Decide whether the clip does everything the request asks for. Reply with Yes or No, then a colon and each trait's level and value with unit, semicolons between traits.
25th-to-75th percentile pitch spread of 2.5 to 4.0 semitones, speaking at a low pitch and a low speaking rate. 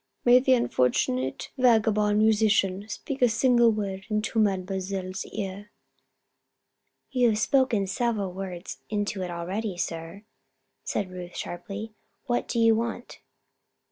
No: average, 3.3 semitones; high, 210 Hz; slow, 120 wpm